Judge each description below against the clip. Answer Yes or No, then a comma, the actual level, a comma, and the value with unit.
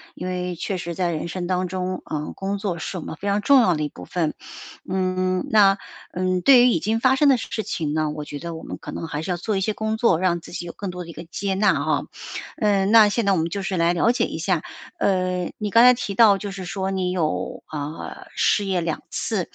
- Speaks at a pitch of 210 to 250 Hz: No, medium, 185 Hz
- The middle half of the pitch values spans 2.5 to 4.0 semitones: Yes, average, 3.0 semitones